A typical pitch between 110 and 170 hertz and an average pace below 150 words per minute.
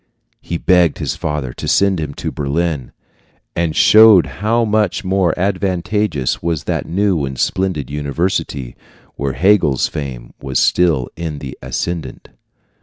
No: very low, 85 Hz; slow, 135 wpm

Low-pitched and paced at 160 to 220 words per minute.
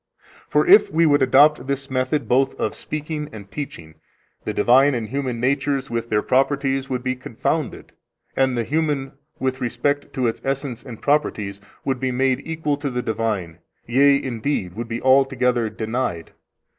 Yes: low, 130 Hz; average, 165 wpm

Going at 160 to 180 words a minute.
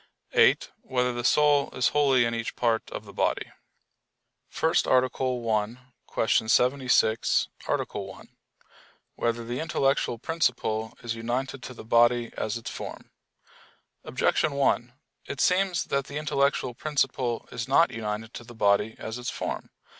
No: average, 145 wpm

